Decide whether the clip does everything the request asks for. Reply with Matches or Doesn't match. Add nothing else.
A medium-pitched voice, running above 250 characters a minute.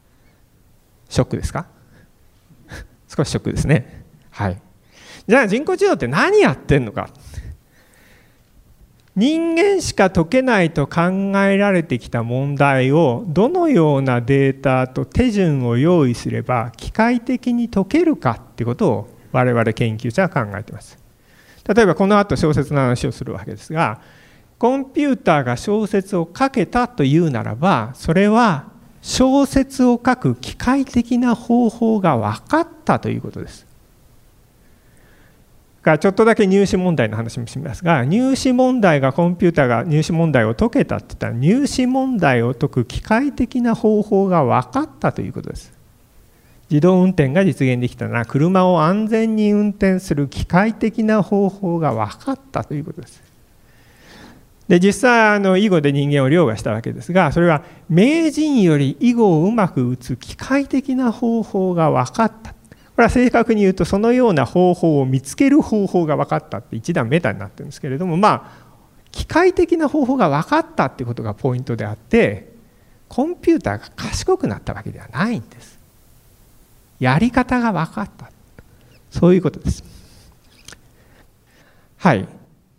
Matches